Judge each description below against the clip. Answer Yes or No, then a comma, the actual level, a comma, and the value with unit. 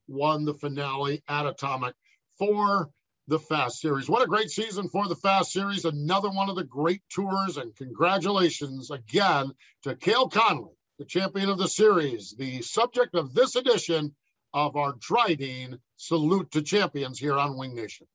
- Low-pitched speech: No, medium, 155 Hz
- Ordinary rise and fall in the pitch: No, wide, 5.7 semitones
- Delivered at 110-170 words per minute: Yes, average, 160 wpm